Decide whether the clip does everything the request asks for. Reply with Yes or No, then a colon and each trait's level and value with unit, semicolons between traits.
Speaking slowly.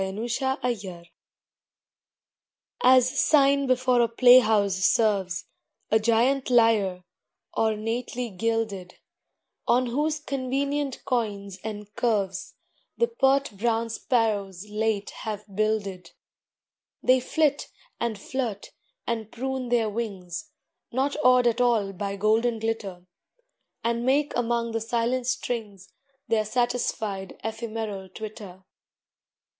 Yes: slow, 110 wpm